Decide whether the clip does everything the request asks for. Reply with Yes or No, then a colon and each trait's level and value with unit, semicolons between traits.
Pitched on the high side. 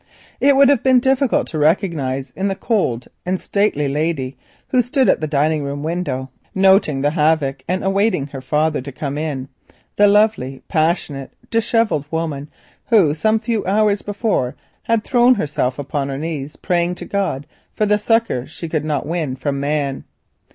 No: medium, 160 Hz